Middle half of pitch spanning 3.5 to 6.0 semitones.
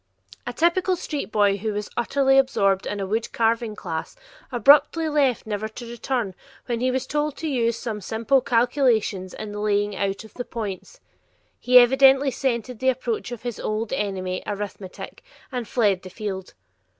Yes: average, 4.1 semitones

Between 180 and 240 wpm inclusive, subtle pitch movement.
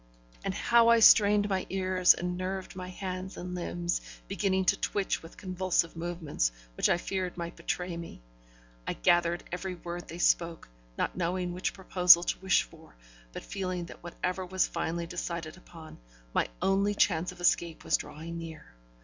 No: average, 165 wpm; narrow, 1.9 semitones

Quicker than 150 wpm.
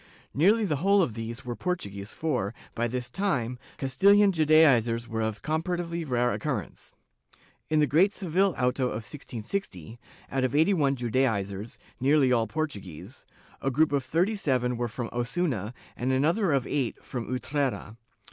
Yes: average, 160 wpm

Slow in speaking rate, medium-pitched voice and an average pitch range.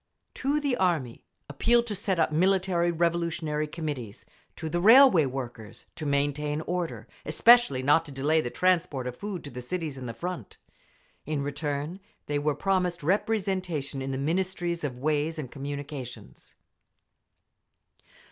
No: average, 145 wpm; medium, 155 Hz; average, 4.4 semitones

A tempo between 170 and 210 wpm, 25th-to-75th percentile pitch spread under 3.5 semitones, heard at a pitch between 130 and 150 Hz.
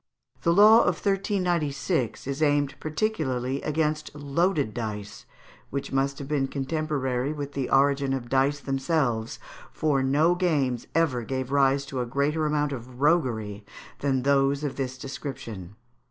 No: average, 140 wpm; average, 2.7 semitones; medium, 140 Hz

